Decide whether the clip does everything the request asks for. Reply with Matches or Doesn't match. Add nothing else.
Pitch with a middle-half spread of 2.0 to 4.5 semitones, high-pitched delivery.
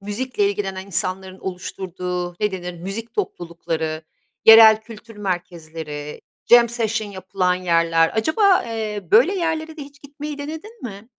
Doesn't match